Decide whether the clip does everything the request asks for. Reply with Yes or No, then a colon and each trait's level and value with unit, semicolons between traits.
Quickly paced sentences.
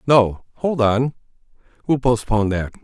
No: slow, 125 wpm